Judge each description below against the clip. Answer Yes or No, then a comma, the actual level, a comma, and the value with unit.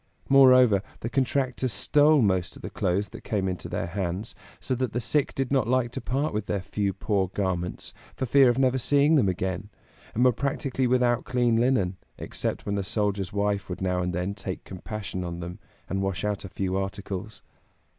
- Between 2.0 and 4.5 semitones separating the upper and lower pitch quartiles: No, average, 5.1 semitones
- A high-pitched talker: No, low, 105 Hz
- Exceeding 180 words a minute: Yes, average, 195 wpm